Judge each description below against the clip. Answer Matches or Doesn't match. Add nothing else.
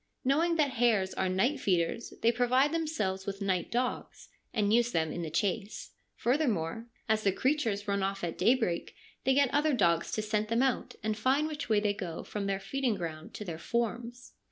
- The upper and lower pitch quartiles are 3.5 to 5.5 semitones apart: Matches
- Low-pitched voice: Doesn't match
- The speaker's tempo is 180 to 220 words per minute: Matches